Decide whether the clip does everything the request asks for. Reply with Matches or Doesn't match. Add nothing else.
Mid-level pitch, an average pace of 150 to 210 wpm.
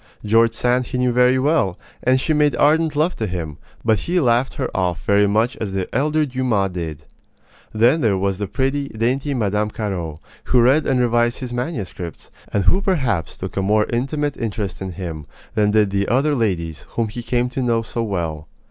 Doesn't match